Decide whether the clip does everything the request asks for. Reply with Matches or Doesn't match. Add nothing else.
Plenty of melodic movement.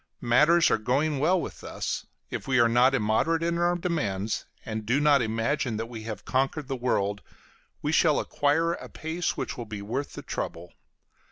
Matches